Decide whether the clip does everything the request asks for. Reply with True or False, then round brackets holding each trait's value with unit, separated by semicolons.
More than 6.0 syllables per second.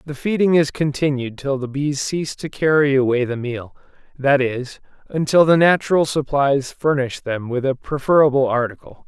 False (4.9 syllables/s)